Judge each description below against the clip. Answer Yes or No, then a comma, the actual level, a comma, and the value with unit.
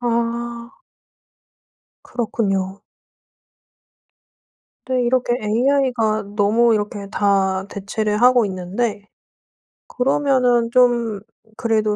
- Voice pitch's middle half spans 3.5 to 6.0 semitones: No, average, 2.8 semitones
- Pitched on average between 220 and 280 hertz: Yes, high, 230 Hz